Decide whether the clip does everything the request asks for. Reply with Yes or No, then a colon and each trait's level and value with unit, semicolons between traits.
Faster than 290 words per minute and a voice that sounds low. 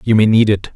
Yes: fast, 315 wpm; low, 105 Hz